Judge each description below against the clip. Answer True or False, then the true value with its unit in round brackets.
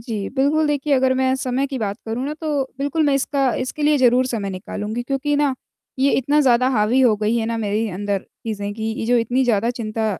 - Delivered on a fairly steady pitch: False (3.8 semitones)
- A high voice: True (250 Hz)